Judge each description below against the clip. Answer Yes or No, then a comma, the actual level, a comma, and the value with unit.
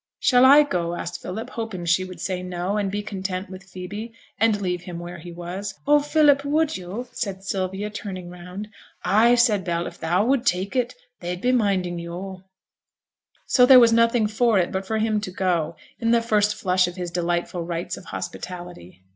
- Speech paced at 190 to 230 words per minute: Yes, average, 195 wpm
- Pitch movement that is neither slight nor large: Yes, average, 4.2 semitones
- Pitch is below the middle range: No, high, 190 Hz